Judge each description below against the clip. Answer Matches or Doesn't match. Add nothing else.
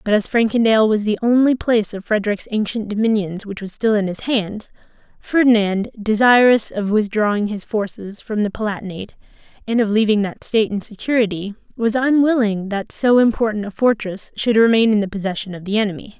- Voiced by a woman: Matches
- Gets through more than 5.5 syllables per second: Matches